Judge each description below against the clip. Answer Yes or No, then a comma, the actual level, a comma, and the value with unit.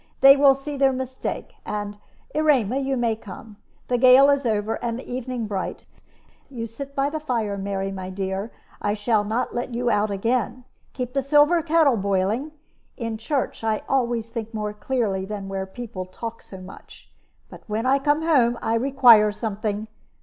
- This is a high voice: Yes, high, 230 Hz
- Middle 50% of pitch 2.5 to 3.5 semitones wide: No, average, 4.3 semitones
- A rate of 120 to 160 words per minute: No, average, 175 wpm